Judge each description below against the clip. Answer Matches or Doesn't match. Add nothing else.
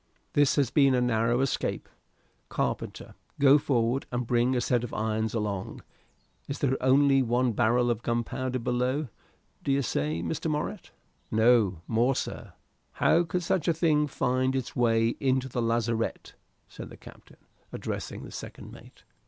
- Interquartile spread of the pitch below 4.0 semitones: Matches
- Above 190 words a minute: Doesn't match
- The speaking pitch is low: Matches